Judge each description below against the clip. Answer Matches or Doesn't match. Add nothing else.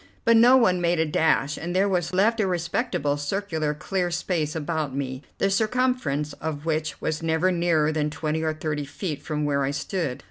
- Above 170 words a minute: Matches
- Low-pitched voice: Doesn't match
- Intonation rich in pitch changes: Doesn't match